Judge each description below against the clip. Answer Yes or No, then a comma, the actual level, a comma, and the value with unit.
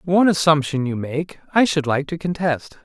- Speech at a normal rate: Yes, average, 190 wpm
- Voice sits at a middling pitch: Yes, medium, 155 Hz